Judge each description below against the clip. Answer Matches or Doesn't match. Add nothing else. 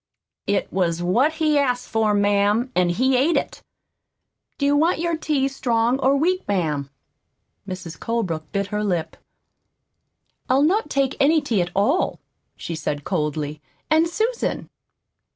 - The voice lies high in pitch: Matches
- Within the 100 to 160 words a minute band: Matches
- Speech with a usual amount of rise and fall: Doesn't match